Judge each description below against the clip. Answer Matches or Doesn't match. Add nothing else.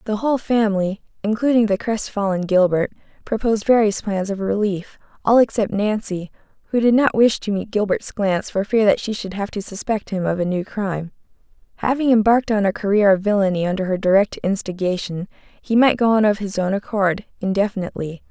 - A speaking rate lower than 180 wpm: Doesn't match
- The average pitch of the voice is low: Doesn't match